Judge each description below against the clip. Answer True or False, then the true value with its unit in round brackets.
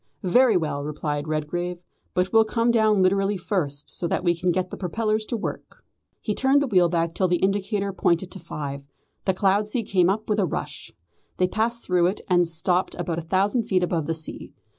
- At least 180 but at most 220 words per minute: True (205 wpm)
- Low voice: False (185 Hz)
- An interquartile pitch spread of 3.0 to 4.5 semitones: True (3.6 semitones)